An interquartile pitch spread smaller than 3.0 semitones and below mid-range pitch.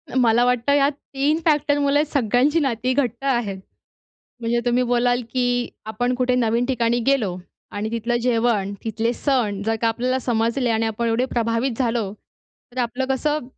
No: narrow, 2.4 semitones; high, 245 Hz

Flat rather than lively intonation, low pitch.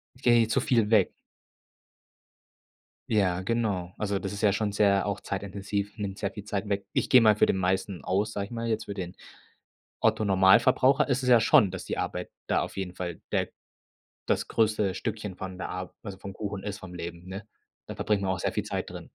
Yes: narrow, 2.3 semitones; low, 100 Hz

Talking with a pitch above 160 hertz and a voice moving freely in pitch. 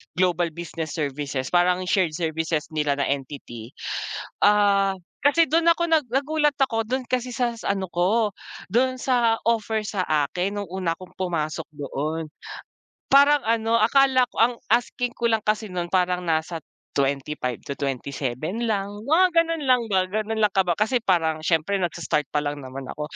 Yes: medium, 185 Hz; wide, 6.9 semitones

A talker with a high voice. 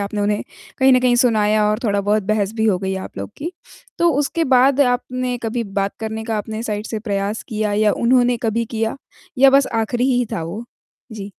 Yes: high, 220 Hz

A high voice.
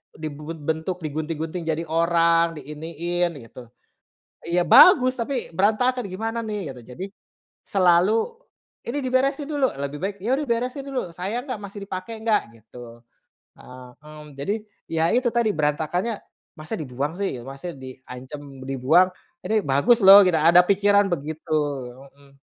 No: medium, 175 Hz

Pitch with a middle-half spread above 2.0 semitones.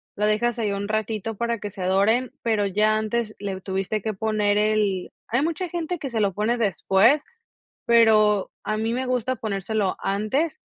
Yes: narrow, 2.5 semitones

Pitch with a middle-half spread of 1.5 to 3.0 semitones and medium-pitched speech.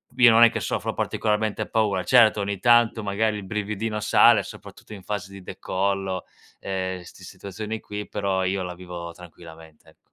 No: narrow, 2.6 semitones; low, 100 Hz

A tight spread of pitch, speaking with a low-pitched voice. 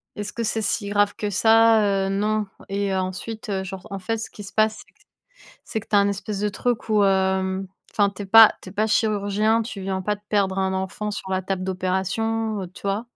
No: narrow, 2.1 semitones; high, 200 Hz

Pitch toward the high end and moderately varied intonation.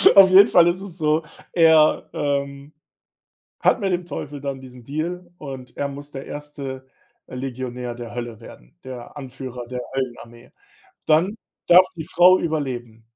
No: medium, 140 Hz; average, 4.4 semitones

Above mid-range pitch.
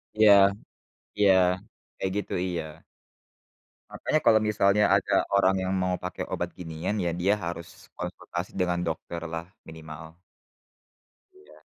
No: very low, 90 Hz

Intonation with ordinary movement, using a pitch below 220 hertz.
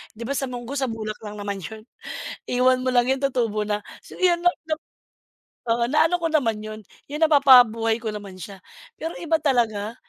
No: average, 4.6 semitones; high, 240 Hz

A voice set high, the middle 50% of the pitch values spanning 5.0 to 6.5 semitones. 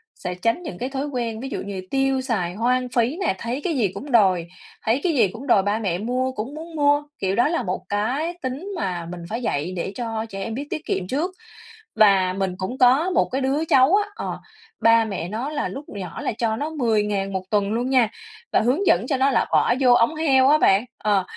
Yes: high, 240 Hz; average, 5.3 semitones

